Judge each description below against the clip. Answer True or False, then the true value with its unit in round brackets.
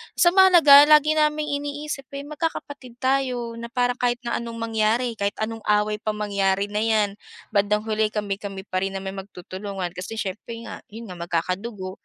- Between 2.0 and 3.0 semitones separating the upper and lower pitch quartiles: False (4.2 semitones)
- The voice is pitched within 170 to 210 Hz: False (220 Hz)